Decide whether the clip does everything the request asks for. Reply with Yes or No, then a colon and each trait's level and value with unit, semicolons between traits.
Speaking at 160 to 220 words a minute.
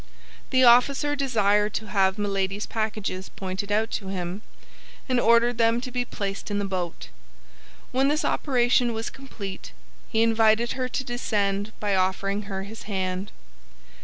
No: average, 150 wpm